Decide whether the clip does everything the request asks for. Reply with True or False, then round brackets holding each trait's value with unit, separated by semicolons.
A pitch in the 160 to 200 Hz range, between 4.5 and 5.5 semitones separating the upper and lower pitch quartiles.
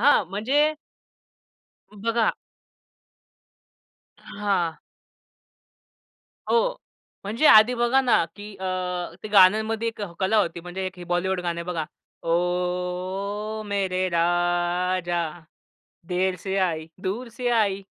False (190 Hz; 3.4 semitones)